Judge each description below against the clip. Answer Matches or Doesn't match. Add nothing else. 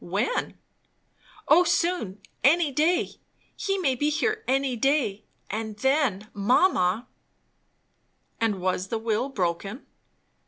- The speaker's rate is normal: Doesn't match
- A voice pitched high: Matches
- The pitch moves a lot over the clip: Matches